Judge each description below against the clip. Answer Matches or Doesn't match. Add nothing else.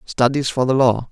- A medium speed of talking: Doesn't match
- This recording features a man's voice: Matches